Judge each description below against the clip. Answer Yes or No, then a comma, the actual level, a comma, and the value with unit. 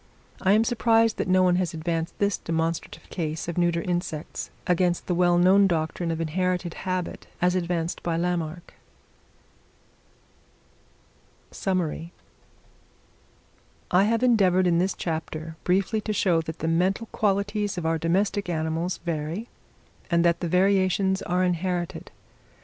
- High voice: No, medium, 180 Hz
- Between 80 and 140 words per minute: Yes, slow, 135 wpm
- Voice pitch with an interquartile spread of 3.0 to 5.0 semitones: No, narrow, 2.4 semitones